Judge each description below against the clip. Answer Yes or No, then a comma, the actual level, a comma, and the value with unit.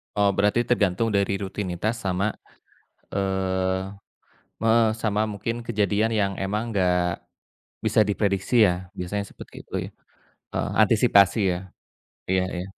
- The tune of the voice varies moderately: No, narrow, 2.3 semitones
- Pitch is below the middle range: Yes, low, 100 Hz